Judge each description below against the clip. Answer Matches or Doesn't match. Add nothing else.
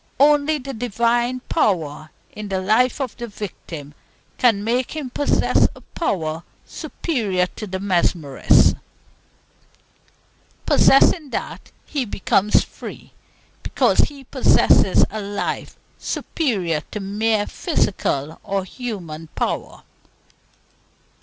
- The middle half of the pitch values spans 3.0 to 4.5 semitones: Doesn't match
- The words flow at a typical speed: Doesn't match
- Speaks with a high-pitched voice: Matches